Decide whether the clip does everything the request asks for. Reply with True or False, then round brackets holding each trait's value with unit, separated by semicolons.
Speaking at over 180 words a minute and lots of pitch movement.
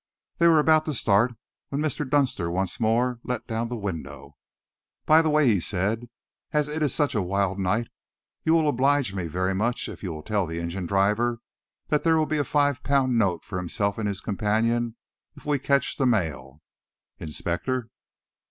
True (190 wpm; 6.7 semitones)